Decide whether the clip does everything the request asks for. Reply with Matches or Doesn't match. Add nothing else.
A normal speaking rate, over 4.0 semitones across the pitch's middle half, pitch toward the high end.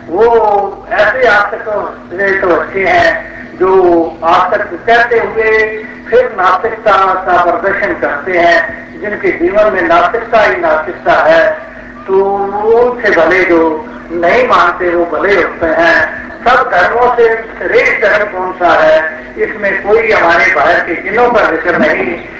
Matches